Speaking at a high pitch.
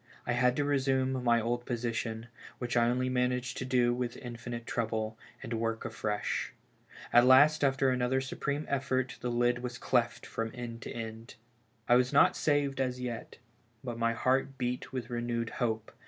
No: low, 125 Hz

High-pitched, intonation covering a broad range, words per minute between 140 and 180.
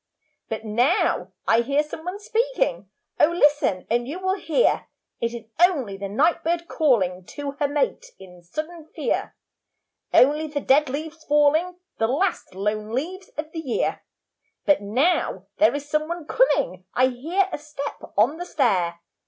Yes: very high, 290 Hz; wide, 6.3 semitones; average, 160 wpm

